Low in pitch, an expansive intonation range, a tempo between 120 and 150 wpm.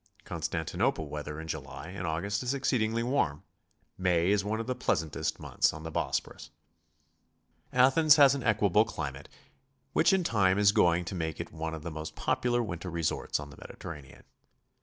No: very low, 90 Hz; wide, 6.3 semitones; average, 170 wpm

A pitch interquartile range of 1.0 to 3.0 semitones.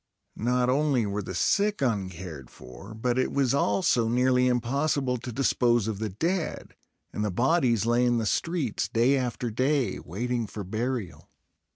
No: average, 3.6 semitones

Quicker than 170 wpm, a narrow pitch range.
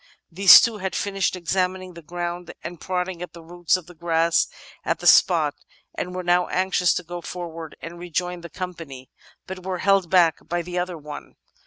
Yes: average, 190 wpm; narrow, 1.5 semitones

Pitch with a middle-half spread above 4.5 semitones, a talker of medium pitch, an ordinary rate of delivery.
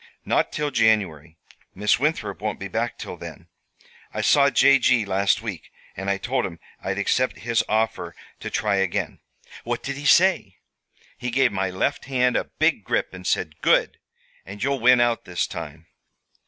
No: average, 5.0 semitones; low, 110 Hz; average, 175 wpm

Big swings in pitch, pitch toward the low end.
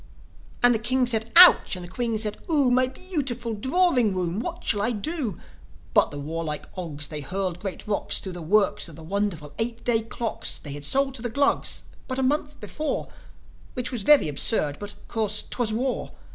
No: wide, 5.9 semitones; high, 220 Hz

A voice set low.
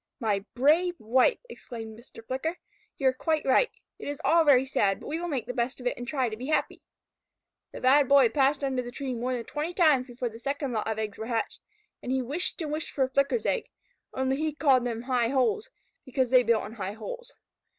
No: very high, 260 Hz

